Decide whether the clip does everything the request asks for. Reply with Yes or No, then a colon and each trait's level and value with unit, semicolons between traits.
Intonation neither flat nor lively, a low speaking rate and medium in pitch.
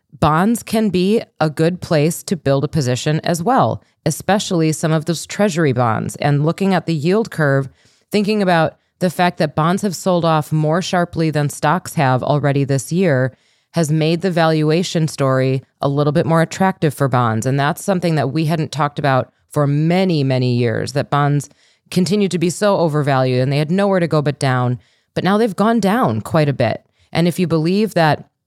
No: average, 4.1 semitones; average, 195 wpm; medium, 160 Hz